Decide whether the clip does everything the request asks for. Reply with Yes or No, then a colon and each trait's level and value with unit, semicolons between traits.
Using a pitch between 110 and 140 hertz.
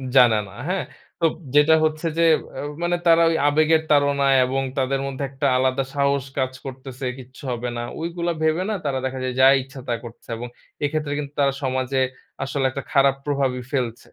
Yes: low, 135 Hz